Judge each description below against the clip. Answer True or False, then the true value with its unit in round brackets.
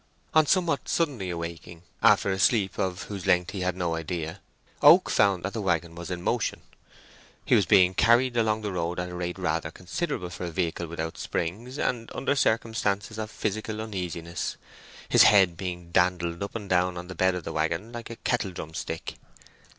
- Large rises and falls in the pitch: False (4.0 semitones)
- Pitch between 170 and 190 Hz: False (90 Hz)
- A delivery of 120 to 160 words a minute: False (190 wpm)